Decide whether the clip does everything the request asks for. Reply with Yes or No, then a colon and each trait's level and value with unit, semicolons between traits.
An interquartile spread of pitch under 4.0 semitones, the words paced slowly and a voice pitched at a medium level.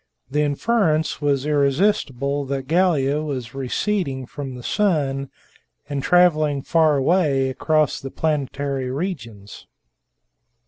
Yes: average, 2.8 semitones; slow, 105 wpm; medium, 145 Hz